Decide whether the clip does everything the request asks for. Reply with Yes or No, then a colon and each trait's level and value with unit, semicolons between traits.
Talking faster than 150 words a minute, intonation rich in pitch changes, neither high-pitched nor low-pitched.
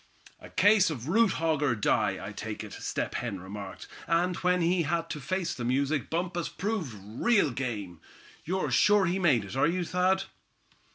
Yes: average, 180 wpm; wide, 7.8 semitones; medium, 160 Hz